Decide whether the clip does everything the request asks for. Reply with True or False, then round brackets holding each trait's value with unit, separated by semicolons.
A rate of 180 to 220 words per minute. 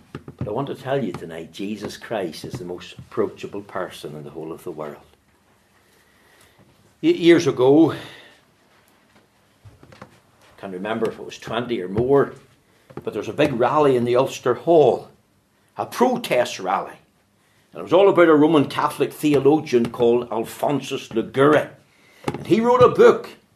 False (160 wpm)